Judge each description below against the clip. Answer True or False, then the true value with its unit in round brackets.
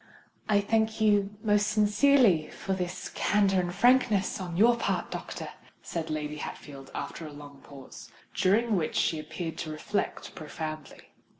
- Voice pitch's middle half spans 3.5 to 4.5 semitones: False (5.1 semitones)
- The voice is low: False (185 Hz)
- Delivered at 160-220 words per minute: False (145 wpm)